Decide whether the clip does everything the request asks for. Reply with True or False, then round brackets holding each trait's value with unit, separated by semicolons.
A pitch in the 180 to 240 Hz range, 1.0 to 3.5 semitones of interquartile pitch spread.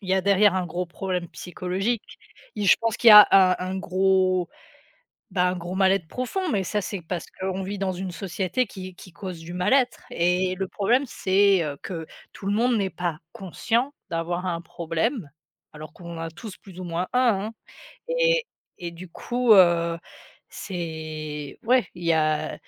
True (185 Hz; 3.1 semitones)